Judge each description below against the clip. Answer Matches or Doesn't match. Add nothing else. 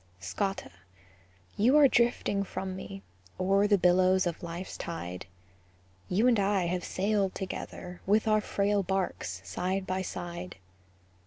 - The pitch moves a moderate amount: Doesn't match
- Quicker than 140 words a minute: Doesn't match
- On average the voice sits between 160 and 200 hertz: Matches